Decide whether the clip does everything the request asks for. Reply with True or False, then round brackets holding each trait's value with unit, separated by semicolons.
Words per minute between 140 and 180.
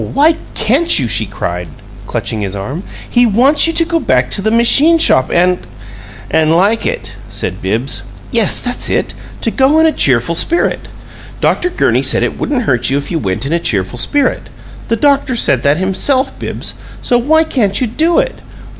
False (190 wpm)